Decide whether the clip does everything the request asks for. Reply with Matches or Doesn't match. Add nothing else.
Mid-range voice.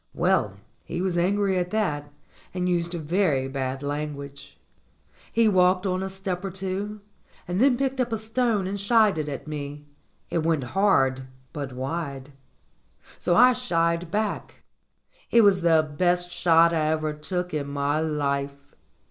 Matches